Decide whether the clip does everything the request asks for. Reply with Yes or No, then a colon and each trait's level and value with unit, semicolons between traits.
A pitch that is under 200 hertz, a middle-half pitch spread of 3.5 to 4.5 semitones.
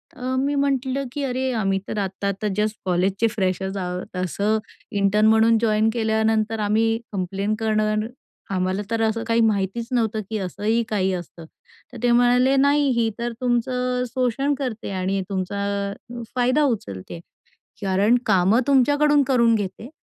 No: high, 220 Hz; average, 3.8 semitones